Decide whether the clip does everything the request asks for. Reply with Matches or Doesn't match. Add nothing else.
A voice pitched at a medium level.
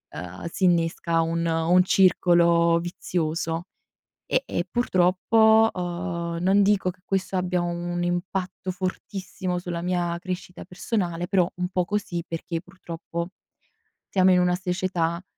Matches